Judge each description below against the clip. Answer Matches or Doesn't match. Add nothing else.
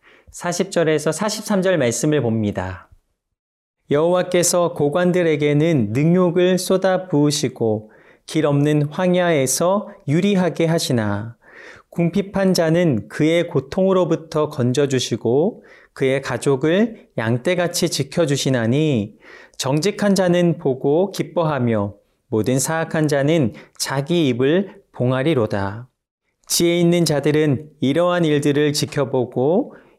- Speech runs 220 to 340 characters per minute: Matches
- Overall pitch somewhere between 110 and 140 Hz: Doesn't match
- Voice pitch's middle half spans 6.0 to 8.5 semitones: Doesn't match